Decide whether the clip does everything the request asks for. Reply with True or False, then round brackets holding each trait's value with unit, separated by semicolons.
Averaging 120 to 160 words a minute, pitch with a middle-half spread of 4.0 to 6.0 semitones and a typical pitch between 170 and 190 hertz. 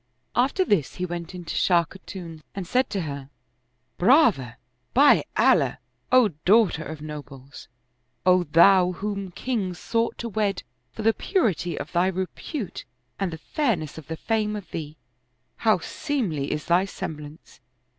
True (155 wpm; 5.3 semitones; 185 Hz)